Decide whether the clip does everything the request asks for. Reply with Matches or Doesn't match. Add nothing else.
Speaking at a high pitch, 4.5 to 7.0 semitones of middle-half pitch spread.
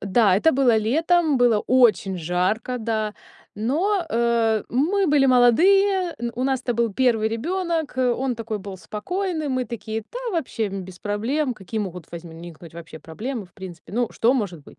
Matches